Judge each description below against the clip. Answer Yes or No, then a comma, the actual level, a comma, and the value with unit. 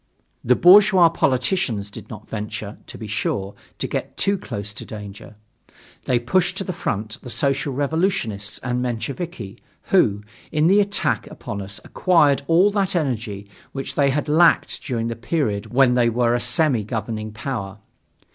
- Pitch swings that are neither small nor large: No, wide, 7.0 semitones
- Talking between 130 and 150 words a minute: No, average, 160 wpm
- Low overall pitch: Yes, low, 125 Hz